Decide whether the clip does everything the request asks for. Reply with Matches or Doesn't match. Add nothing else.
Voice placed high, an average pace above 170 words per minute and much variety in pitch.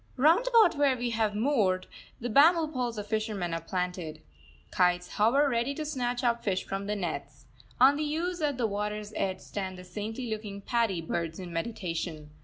Matches